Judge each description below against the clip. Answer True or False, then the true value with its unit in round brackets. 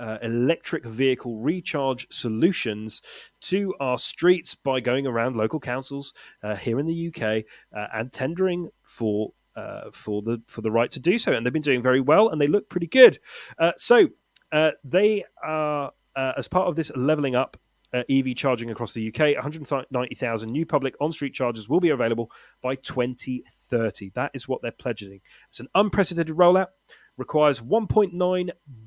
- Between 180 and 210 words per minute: False (170 wpm)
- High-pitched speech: False (135 Hz)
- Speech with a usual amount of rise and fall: False (5.7 semitones)